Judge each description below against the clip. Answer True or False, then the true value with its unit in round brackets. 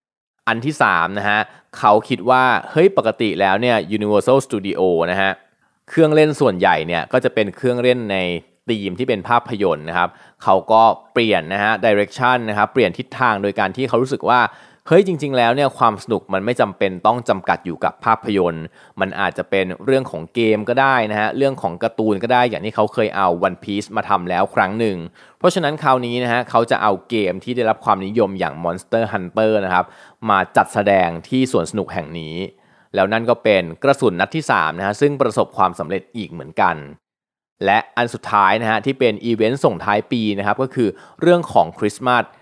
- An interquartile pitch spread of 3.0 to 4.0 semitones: False (4.5 semitones)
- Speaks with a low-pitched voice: True (110 Hz)